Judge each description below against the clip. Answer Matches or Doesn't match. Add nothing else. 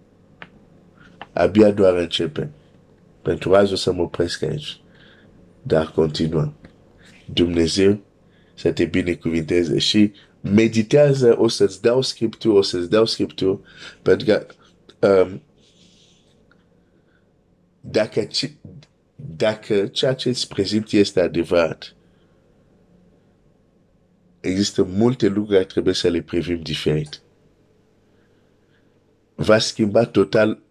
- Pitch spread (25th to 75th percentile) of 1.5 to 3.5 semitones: Doesn't match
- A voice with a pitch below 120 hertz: Matches